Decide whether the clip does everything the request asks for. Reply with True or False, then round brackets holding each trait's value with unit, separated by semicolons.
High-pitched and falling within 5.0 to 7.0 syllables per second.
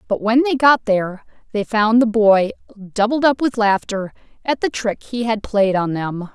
False (215 Hz; 4.5 syllables/s)